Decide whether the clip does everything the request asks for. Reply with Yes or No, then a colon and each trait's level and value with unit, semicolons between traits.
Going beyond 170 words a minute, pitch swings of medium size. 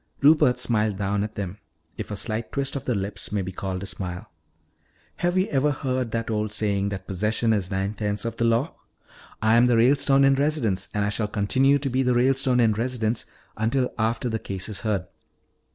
Yes: fast, 205 wpm; average, 3.9 semitones